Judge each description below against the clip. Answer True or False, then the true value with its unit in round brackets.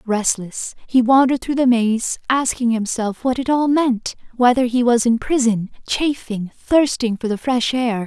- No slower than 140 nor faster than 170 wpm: True (165 wpm)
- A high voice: True (240 Hz)